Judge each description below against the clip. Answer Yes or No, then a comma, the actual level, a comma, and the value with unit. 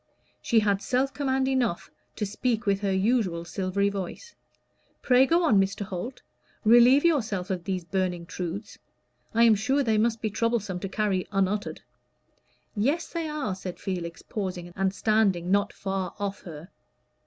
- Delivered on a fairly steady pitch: No, average, 4.0 semitones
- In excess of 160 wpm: No, average, 155 wpm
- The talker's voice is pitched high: Yes, high, 205 Hz